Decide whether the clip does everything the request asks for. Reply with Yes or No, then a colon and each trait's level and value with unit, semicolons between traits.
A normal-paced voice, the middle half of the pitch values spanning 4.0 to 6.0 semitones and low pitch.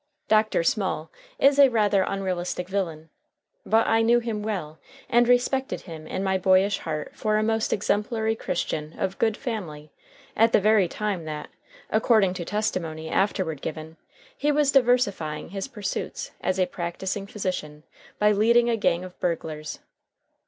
No: average, 150 wpm; average, 4.6 semitones; high, 195 Hz